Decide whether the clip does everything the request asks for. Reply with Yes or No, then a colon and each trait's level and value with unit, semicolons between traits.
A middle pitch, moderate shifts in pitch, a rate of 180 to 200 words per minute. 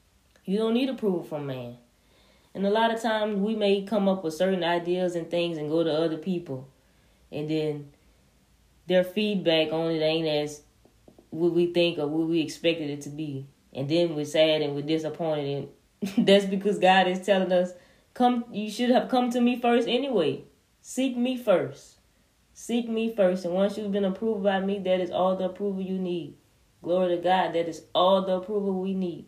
Yes: medium, 180 Hz; average, 4.5 semitones; average, 195 wpm